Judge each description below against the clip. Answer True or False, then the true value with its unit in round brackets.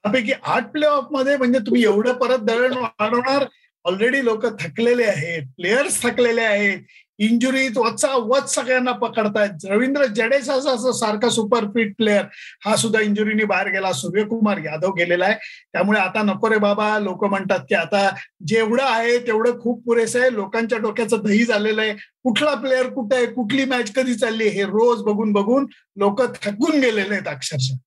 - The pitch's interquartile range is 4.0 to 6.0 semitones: False (3.5 semitones)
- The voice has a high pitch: True (225 Hz)